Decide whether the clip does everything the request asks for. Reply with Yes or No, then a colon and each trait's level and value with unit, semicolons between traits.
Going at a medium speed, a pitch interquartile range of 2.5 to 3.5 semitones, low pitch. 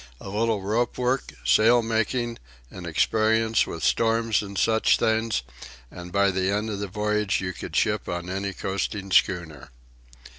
Yes: average, 155 wpm; average, 3.0 semitones; low, 105 Hz